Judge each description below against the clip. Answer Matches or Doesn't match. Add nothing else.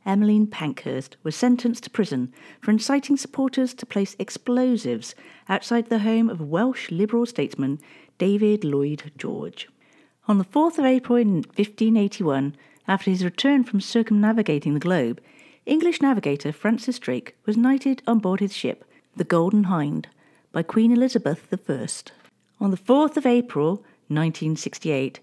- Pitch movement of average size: Doesn't match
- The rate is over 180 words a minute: Doesn't match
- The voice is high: Matches